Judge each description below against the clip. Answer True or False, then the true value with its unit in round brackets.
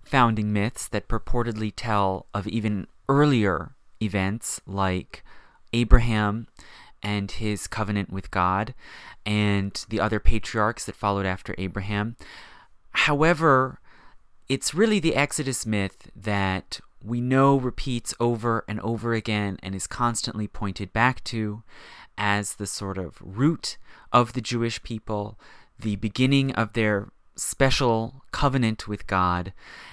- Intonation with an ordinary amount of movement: True (3.0 semitones)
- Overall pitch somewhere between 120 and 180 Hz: False (110 Hz)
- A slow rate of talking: True (120 wpm)